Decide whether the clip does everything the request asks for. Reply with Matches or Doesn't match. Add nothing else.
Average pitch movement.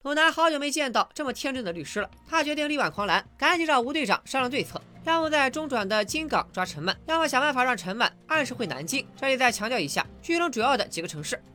Doesn't match